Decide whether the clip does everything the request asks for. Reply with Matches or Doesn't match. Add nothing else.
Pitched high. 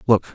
Doesn't match